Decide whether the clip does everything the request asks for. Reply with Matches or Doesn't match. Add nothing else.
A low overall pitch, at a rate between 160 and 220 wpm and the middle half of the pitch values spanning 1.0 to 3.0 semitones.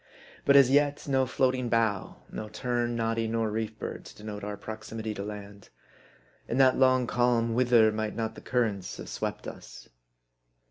Matches